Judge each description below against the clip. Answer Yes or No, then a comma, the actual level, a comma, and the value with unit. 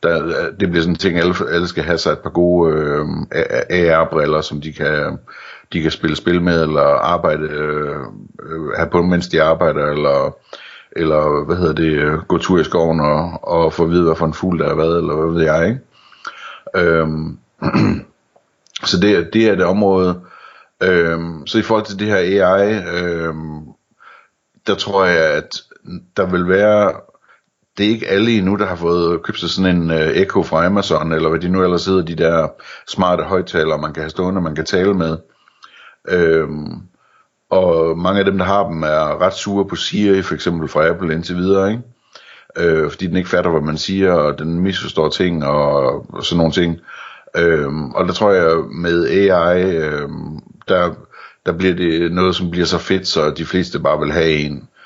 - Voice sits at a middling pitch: No, very low, 85 Hz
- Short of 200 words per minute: Yes, average, 190 wpm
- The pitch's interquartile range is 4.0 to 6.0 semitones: No, average, 2.7 semitones